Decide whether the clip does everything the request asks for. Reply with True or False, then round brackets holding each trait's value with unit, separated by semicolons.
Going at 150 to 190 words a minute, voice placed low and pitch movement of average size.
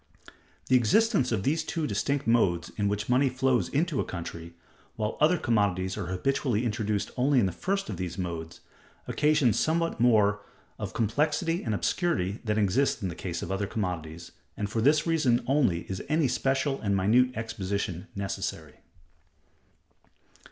False (160 wpm; 110 Hz; 6.3 semitones)